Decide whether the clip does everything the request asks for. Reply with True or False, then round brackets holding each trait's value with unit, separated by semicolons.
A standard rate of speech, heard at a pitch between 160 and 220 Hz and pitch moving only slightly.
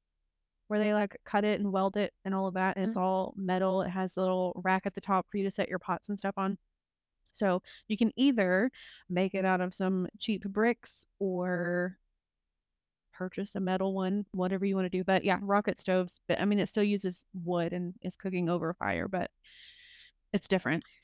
False (210 wpm; 190 Hz; 1.7 semitones)